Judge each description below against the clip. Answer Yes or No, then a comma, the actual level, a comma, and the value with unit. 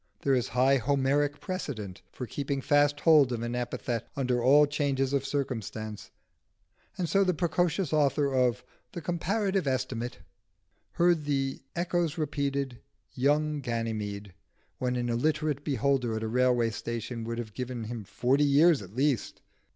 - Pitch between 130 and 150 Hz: Yes, low, 135 Hz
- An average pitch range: Yes, average, 3.7 semitones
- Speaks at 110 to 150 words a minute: Yes, average, 145 wpm